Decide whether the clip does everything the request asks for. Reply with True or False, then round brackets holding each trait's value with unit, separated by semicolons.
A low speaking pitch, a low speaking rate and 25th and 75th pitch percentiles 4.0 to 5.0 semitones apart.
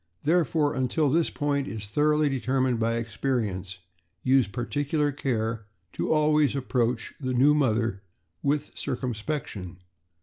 True (130 Hz; 125 wpm; 4.3 semitones)